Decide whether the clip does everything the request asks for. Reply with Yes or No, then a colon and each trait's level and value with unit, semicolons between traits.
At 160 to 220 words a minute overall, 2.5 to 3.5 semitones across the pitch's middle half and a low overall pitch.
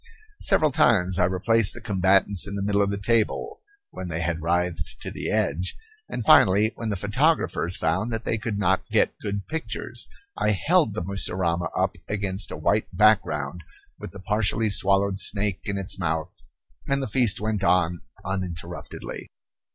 Yes: average, 165 wpm; average, 3.2 semitones; low, 100 Hz